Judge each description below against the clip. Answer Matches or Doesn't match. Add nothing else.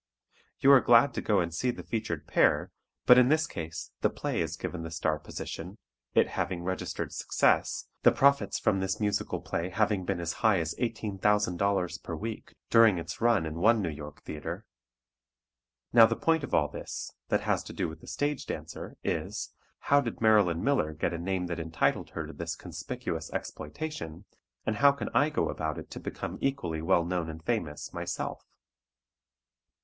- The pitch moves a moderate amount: Doesn't match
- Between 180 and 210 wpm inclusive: Matches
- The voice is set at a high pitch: Doesn't match